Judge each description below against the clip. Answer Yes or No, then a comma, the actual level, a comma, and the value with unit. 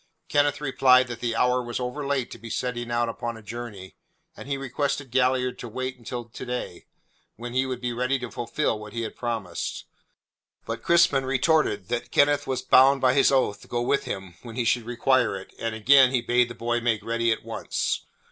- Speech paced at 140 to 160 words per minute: No, fast, 205 wpm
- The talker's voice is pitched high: No, low, 125 Hz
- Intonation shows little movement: Yes, narrow, 2.1 semitones